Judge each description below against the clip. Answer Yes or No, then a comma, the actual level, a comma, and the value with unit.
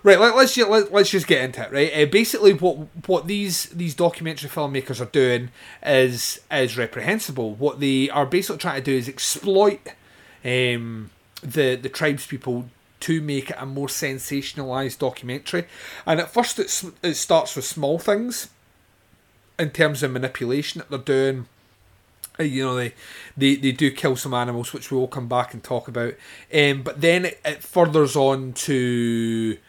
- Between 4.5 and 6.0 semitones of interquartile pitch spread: Yes, average, 4.8 semitones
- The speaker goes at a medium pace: Yes, average, 170 wpm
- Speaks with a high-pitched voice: No, medium, 140 Hz